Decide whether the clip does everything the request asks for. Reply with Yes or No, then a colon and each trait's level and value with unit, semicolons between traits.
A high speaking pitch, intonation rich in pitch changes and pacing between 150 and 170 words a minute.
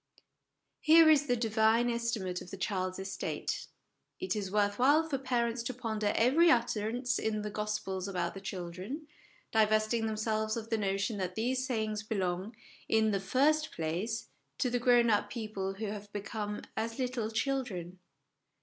No: high, 220 Hz; average, 3.3 semitones; average, 160 wpm